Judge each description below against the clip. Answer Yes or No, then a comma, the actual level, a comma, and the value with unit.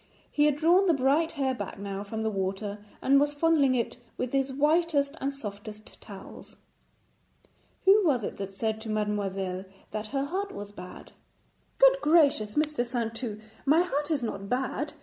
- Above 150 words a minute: Yes, average, 170 wpm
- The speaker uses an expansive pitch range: Yes, wide, 6.1 semitones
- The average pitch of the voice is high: Yes, very high, 260 Hz